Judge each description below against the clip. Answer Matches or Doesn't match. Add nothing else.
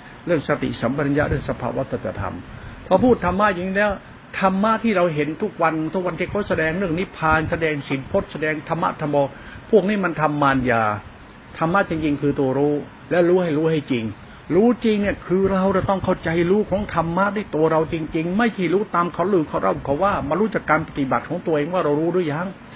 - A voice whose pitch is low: Doesn't match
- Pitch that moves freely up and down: Doesn't match